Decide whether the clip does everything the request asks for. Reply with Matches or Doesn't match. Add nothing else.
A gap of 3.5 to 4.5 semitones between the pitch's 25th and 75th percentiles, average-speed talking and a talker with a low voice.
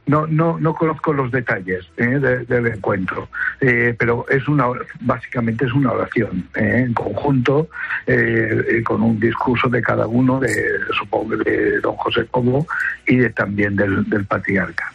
Matches